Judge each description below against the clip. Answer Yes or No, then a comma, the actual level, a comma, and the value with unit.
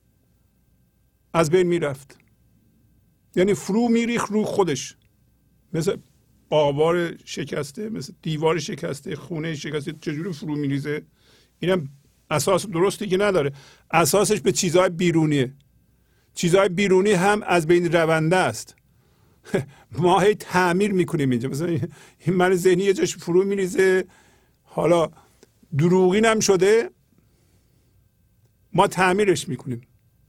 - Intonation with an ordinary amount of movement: Yes, average, 4.8 semitones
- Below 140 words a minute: Yes, average, 110 wpm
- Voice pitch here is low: No, medium, 175 Hz